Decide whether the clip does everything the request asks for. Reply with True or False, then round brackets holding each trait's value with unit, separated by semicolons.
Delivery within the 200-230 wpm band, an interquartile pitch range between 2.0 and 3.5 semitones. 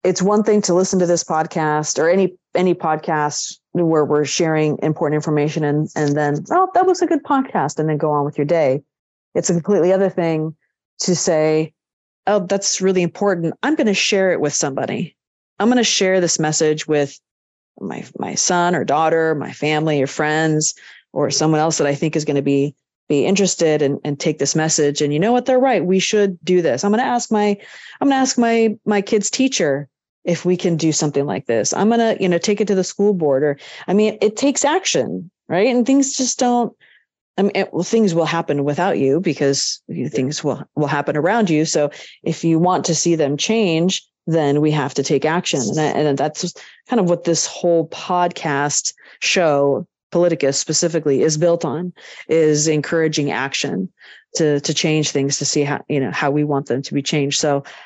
False (205 wpm; 4.6 semitones)